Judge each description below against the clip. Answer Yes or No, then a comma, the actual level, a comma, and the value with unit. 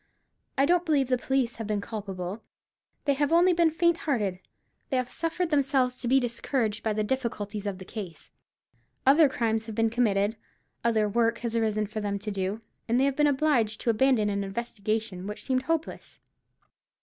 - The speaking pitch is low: No, high, 230 Hz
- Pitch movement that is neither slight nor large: Yes, average, 4.3 semitones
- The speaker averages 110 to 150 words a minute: No, average, 185 wpm